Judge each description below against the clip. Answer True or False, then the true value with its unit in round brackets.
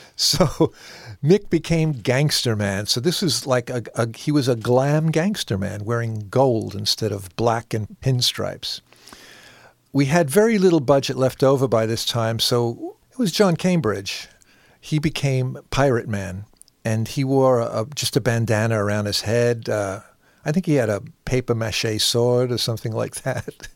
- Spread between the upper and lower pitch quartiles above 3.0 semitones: True (4.5 semitones)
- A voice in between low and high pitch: False (125 Hz)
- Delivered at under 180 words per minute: True (165 wpm)